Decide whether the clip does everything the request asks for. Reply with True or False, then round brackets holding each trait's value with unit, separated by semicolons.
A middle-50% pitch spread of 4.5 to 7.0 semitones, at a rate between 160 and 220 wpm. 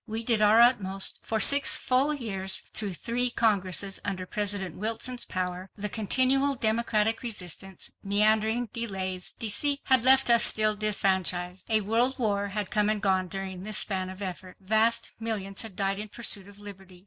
False (3.0 semitones; 165 wpm)